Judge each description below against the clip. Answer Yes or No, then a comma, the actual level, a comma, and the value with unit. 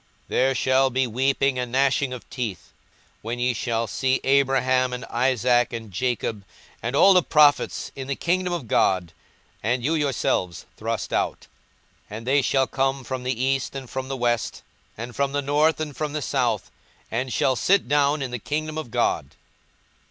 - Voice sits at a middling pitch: No, low, 130 Hz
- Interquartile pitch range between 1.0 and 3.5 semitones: Yes, narrow, 2.4 semitones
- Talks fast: No, average, 180 wpm